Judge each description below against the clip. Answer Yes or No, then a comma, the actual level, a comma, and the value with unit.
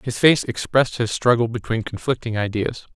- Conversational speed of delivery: Yes, average, 165 wpm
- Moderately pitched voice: No, low, 115 Hz